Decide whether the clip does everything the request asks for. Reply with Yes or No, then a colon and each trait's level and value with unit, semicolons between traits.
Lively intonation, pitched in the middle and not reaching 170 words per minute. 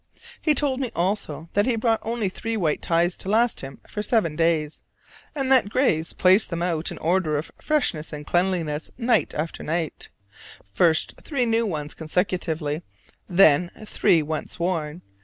Yes: wide, 6.0 semitones; medium, 175 Hz; average, 160 wpm